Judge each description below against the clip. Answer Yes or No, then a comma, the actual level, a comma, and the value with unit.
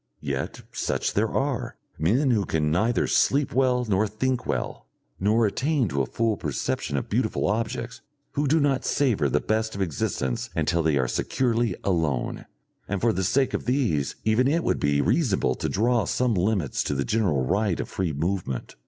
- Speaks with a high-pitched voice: No, low, 105 Hz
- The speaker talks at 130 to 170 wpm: No, average, 180 wpm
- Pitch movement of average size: No, wide, 7.4 semitones